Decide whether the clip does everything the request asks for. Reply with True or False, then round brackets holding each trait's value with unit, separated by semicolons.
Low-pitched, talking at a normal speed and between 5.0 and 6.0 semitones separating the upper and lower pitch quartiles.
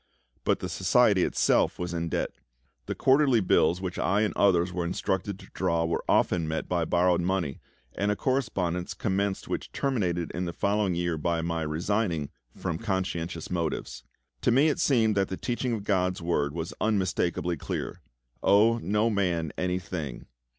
False (90 Hz; 170 wpm; 3.4 semitones)